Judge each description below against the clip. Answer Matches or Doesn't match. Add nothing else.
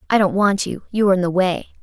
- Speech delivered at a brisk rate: Matches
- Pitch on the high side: Matches